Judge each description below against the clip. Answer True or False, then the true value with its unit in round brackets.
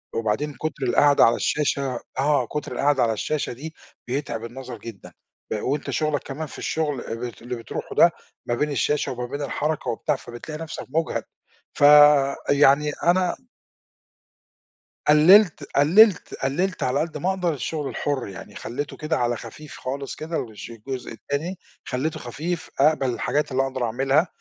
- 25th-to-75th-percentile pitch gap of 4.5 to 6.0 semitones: False (3.4 semitones)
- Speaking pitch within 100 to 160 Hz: True (140 Hz)